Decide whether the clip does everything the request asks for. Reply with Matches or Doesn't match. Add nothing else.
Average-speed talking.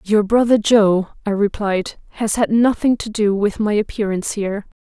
Matches